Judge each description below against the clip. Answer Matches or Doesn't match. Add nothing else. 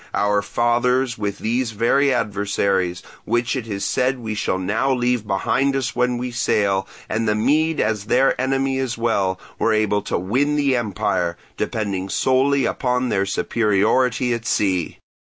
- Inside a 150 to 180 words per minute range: Matches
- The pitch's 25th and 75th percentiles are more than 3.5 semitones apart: Matches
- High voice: Doesn't match